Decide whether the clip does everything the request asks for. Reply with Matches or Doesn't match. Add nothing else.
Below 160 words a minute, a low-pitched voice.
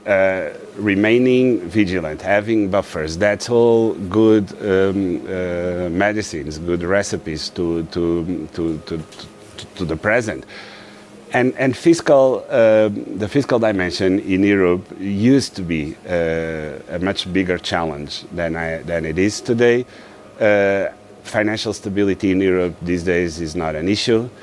Matches